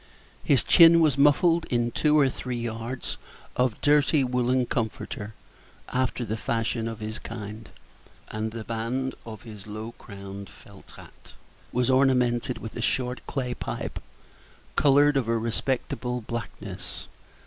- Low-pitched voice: Yes, low, 120 Hz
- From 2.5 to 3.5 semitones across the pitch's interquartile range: Yes, average, 2.9 semitones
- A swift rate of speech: No, slow, 135 wpm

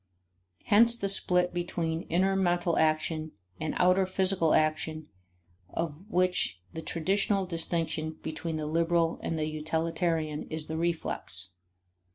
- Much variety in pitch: No, narrow, 2.4 semitones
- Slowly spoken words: Yes, slow, 125 wpm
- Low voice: No, medium, 165 Hz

